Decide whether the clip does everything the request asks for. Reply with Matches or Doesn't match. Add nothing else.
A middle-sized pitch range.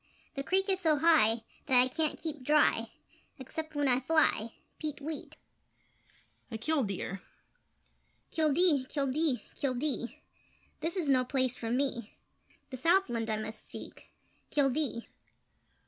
Matches